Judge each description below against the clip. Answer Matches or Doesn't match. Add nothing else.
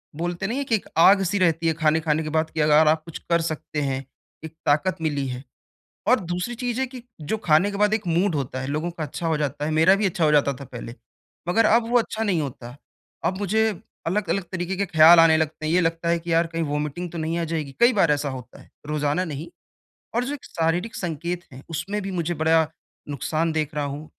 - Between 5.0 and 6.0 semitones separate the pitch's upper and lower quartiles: Doesn't match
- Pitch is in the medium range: Matches